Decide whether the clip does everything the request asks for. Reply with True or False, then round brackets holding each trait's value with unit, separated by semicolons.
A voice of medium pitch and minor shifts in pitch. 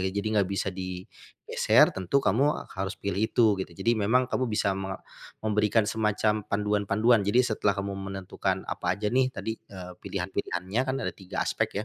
False (100 Hz; 2.3 semitones)